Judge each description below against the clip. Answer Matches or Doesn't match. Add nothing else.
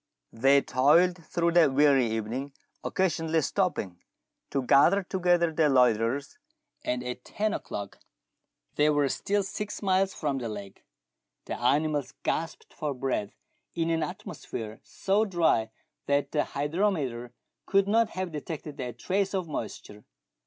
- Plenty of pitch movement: Matches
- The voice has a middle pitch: Matches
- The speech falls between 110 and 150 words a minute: Matches